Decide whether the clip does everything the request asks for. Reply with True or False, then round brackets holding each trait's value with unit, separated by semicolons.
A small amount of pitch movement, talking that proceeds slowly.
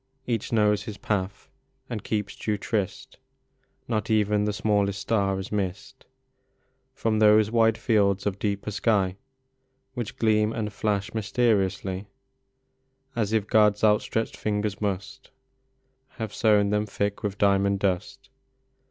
True (1.7 semitones; 130 wpm)